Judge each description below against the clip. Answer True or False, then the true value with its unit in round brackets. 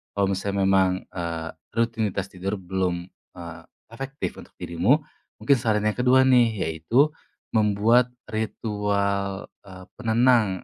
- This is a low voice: True (100 Hz)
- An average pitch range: True (3.6 semitones)